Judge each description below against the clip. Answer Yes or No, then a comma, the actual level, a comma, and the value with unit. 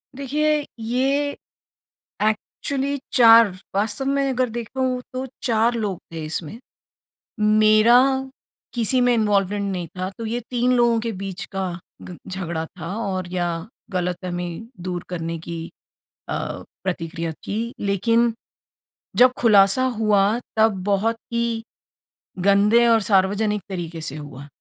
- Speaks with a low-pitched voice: No, high, 210 Hz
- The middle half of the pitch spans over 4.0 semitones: Yes, average, 4.4 semitones